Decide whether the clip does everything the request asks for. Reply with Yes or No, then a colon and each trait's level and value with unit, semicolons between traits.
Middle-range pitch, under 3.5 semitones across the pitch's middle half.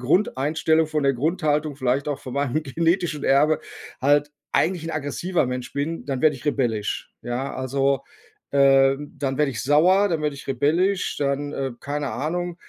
Yes: medium, 145 Hz; average, 2.7 semitones